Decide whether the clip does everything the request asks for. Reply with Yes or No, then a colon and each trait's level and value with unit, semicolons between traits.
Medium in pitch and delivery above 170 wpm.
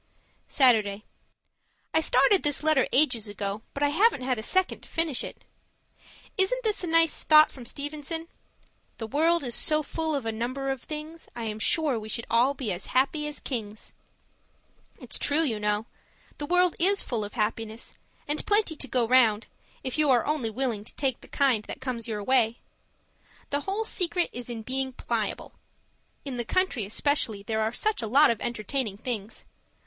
No: very high, 260 Hz; average, 185 wpm